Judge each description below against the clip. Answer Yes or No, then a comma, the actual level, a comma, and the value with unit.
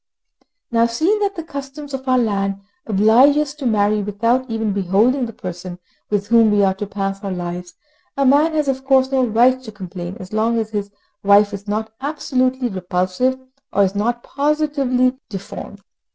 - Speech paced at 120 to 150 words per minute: No, average, 180 wpm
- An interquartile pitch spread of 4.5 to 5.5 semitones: Yes, average, 4.8 semitones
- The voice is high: Yes, high, 225 Hz